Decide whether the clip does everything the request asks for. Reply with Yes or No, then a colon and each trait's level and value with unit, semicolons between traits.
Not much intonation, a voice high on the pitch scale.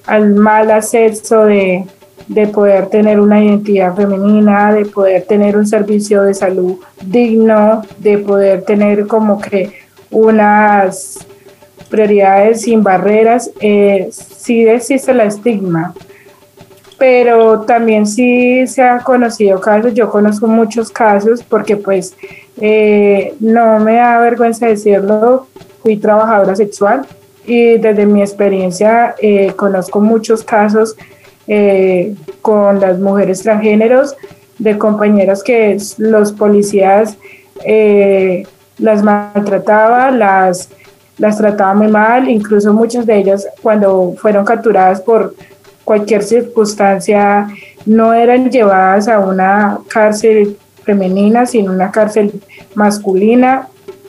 Yes: narrow, 2.0 semitones; high, 210 Hz